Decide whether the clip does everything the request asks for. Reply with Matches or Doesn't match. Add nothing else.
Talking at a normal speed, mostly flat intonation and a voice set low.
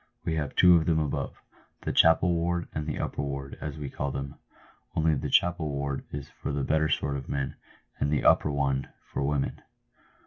Doesn't match